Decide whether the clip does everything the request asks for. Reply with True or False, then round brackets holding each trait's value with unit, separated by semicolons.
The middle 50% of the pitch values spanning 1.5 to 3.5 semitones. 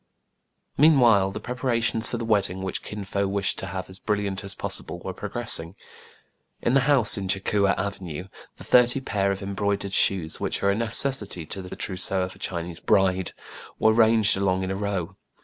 True (2.7 semitones)